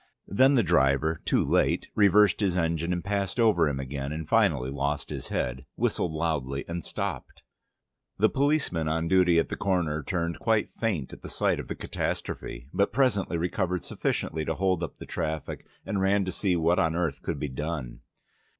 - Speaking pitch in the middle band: No, very low, 85 Hz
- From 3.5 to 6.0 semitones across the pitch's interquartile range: Yes, average, 4.1 semitones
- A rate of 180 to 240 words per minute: Yes, average, 185 wpm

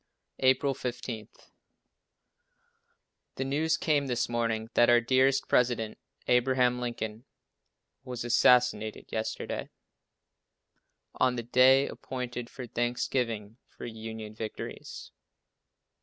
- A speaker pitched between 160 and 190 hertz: No, low, 120 Hz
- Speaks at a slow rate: Yes, slow, 95 wpm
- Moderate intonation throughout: No, narrow, 2.3 semitones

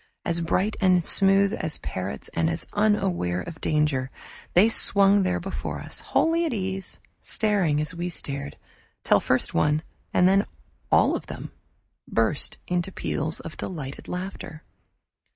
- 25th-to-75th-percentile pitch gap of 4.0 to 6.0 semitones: Yes, average, 4.5 semitones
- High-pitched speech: No, medium, 180 Hz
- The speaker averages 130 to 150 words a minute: Yes, average, 145 wpm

